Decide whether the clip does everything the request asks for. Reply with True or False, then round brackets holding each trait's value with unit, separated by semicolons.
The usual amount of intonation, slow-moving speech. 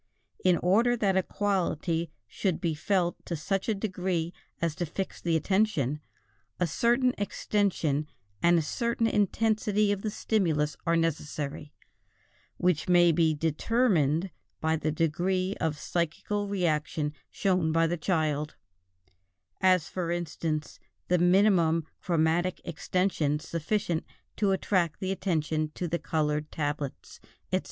True (3.7 semitones; 130 wpm)